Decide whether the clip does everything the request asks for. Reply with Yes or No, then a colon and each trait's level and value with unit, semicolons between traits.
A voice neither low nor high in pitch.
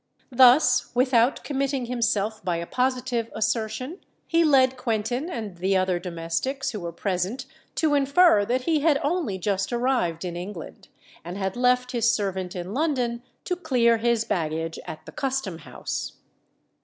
No: high, 235 Hz